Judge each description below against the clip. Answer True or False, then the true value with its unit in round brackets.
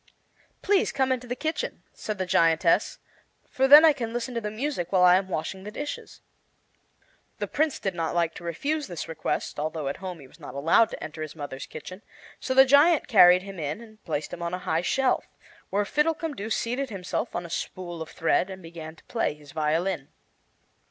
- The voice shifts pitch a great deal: True (7.4 semitones)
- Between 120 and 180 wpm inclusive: False (205 wpm)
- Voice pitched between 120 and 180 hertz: False (190 Hz)